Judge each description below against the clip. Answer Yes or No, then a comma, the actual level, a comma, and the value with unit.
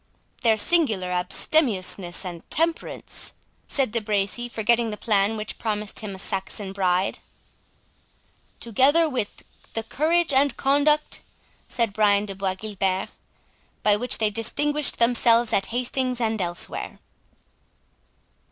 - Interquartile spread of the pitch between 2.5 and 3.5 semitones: No, average, 4.4 semitones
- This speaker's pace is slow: Yes, slow, 120 wpm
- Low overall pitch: No, high, 220 Hz